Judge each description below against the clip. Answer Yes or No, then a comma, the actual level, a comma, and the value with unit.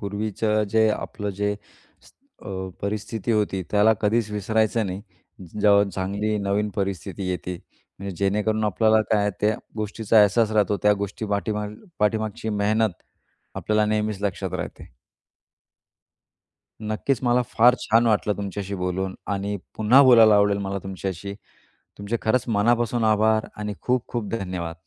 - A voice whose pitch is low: Yes, low, 105 Hz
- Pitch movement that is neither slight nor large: No, narrow, 1.5 semitones